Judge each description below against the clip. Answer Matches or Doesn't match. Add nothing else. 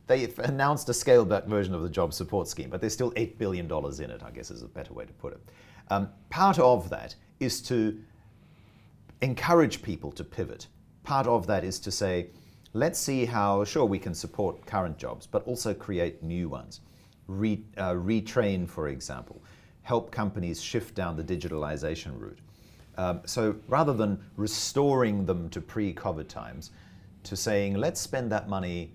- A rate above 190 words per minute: Doesn't match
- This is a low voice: Matches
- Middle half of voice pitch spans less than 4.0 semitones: Doesn't match